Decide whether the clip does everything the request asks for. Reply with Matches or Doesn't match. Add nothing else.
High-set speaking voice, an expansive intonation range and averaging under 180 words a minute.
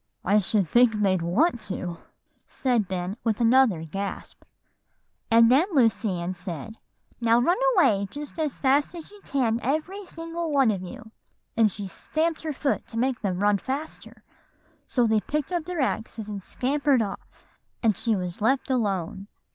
Matches